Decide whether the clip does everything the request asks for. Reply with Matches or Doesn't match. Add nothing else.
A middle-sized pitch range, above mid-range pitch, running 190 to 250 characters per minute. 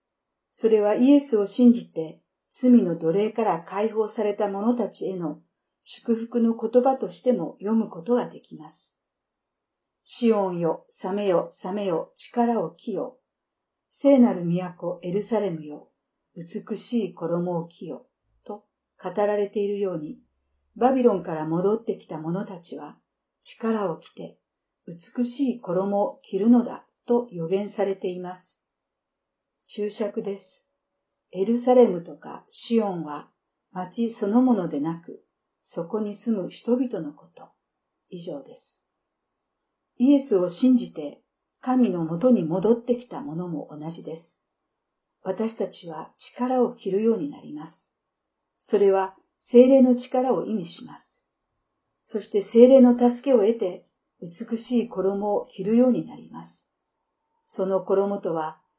Matches